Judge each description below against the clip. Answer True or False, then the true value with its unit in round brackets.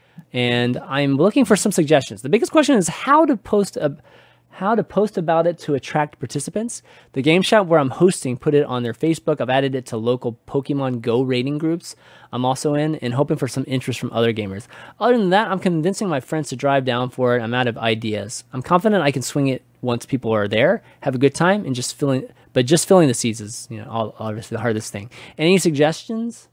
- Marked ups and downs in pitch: True (5.8 semitones)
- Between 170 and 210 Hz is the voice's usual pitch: False (140 Hz)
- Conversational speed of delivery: False (230 wpm)